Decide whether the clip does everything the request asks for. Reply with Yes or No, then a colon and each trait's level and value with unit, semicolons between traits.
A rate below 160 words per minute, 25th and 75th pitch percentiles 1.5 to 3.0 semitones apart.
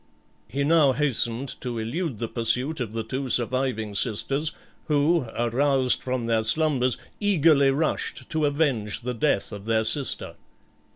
No: average, 140 wpm; average, 4.2 semitones